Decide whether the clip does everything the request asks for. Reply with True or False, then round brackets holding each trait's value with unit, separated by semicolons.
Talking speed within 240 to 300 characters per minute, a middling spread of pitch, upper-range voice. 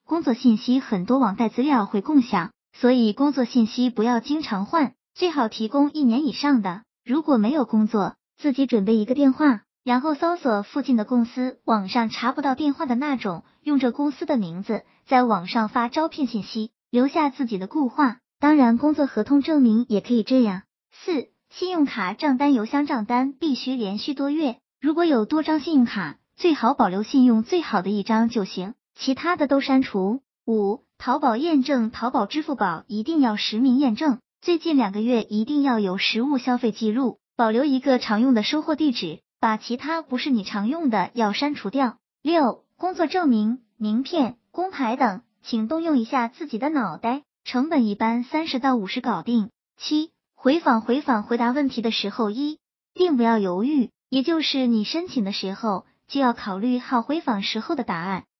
True (275 characters per minute; 4.4 semitones; 250 Hz)